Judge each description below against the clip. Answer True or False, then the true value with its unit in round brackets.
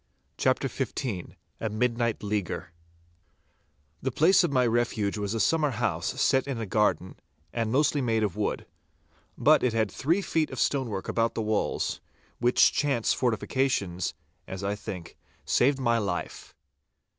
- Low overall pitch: True (115 Hz)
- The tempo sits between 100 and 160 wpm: True (145 wpm)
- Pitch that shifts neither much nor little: True (4.3 semitones)